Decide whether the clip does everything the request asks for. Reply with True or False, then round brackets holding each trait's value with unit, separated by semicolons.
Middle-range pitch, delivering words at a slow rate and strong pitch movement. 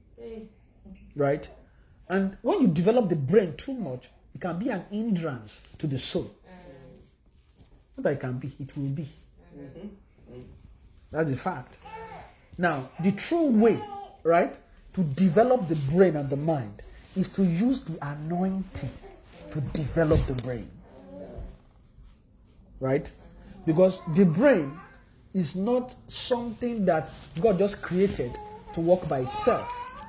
True (175 Hz; 130 wpm; 6.7 semitones)